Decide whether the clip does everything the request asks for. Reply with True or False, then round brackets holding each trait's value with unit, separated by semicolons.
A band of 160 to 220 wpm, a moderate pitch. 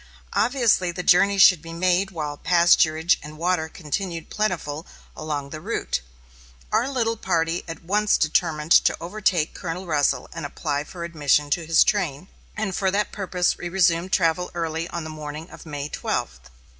True (165 wpm; 170 Hz)